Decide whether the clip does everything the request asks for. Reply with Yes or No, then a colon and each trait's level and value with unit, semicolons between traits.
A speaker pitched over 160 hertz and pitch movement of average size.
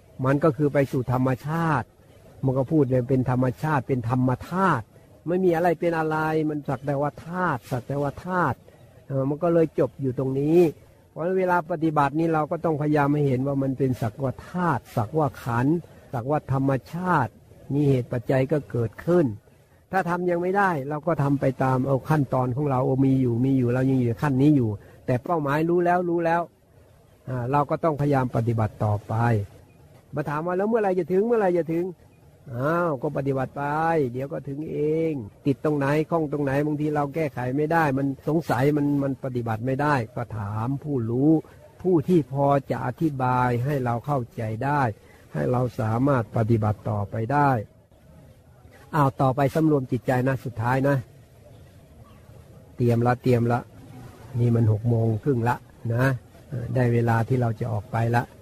No: low, 135 Hz; average, 3.9 semitones